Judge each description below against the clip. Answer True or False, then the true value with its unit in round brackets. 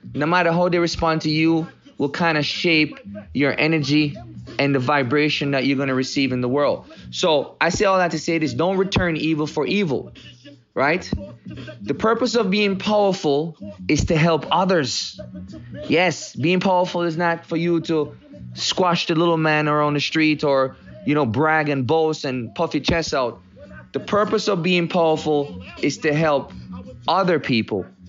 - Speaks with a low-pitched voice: False (155 Hz)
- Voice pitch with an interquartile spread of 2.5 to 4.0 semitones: True (3.5 semitones)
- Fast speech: False (175 wpm)